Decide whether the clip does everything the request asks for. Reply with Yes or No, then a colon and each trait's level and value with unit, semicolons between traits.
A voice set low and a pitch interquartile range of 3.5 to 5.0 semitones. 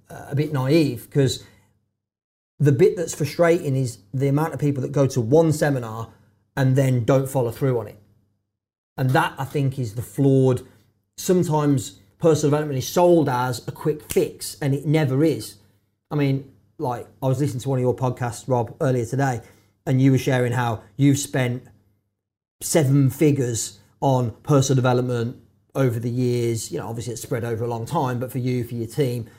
Yes: low, 130 Hz; average, 3.8 semitones